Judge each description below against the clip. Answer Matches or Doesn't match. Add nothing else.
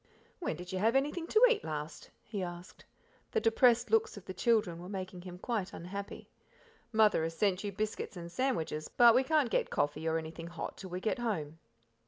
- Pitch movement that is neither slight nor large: Doesn't match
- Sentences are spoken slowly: Doesn't match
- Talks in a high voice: Matches